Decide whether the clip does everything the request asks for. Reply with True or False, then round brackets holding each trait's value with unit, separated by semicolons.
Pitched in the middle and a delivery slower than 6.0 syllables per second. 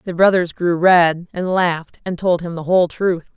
True (175 Hz; 4.9 syllables/s)